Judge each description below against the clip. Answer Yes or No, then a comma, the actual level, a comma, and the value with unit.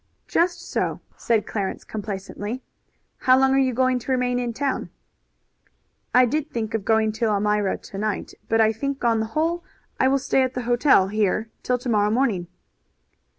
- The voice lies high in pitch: Yes, high, 235 Hz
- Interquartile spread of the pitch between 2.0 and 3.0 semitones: No, average, 3.4 semitones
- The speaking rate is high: No, average, 180 wpm